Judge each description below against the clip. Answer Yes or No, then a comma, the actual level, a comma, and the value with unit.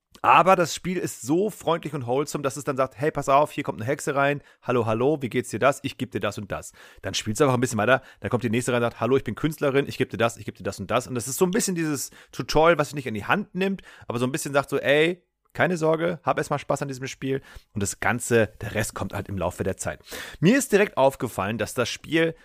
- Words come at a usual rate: No, fast, 290 wpm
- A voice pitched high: No, low, 135 Hz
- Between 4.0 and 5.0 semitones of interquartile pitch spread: Yes, average, 4.6 semitones